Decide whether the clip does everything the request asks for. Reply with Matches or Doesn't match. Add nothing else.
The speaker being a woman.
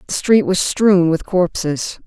Matches